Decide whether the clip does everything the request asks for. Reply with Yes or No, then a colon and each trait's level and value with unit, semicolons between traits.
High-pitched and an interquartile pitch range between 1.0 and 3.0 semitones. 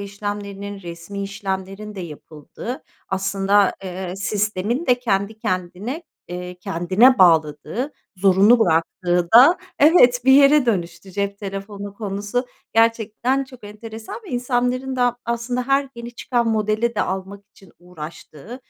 No: high, 205 Hz; average, 4.3 semitones